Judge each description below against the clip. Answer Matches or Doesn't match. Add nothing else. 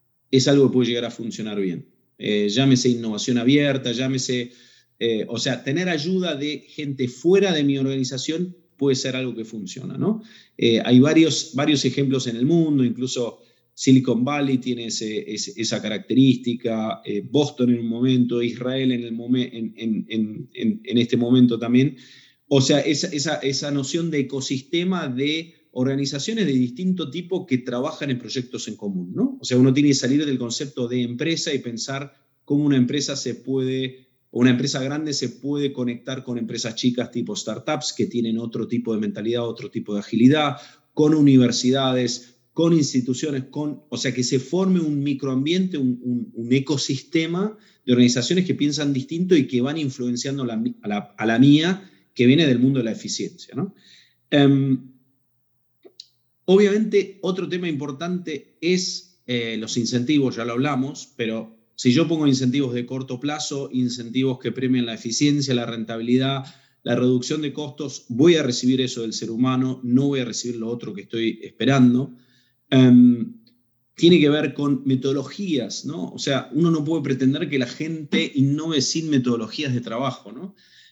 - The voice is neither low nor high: Doesn't match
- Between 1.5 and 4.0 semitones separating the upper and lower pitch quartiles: Matches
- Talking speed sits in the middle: Matches